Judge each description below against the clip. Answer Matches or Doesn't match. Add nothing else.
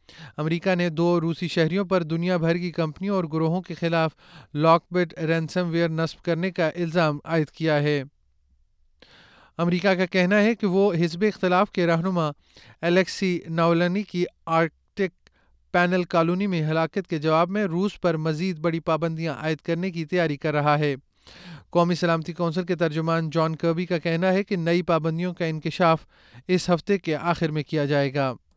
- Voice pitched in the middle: Matches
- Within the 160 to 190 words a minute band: Matches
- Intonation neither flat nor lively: Doesn't match